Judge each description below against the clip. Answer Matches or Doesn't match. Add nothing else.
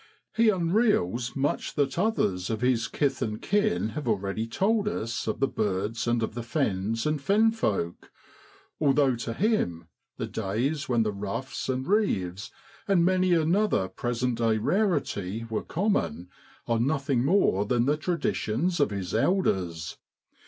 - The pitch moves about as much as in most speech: Doesn't match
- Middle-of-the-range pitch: Doesn't match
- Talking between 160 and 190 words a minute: Doesn't match